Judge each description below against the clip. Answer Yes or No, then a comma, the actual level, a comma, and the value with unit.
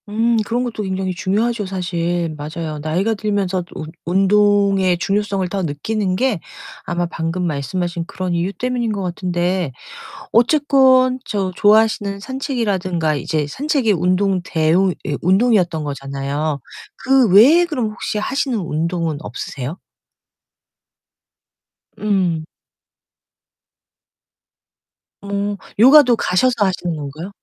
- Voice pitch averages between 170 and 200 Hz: Yes, high, 190 Hz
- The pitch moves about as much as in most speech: Yes, average, 4.3 semitones